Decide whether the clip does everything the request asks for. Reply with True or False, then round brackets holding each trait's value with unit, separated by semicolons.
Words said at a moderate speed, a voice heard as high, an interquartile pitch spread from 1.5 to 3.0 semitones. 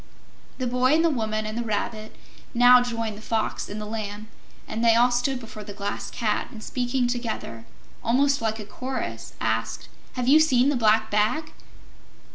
True (180 wpm; 230 Hz; 2.7 semitones)